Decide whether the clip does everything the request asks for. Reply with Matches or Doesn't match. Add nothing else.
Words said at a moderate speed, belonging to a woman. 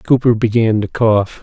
Doesn't match